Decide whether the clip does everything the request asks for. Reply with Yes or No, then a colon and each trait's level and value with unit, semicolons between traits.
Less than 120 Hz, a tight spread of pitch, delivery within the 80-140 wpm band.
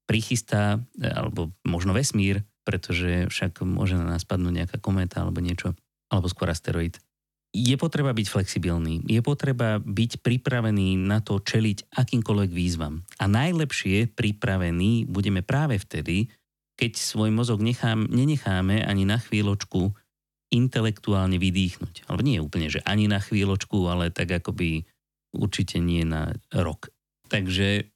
No: low, 100 Hz; average, 3.7 semitones; average, 130 wpm